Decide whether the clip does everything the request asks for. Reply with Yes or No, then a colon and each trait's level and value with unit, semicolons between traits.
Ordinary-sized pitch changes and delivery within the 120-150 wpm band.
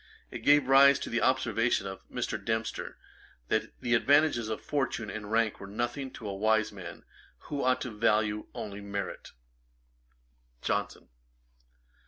Yes: average, 3.7 semitones; average, 145 wpm